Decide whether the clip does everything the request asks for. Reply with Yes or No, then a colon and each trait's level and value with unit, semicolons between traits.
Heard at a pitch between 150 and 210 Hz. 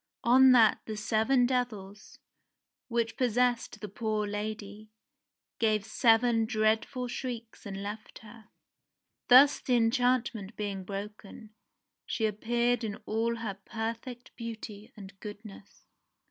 No: high, 225 Hz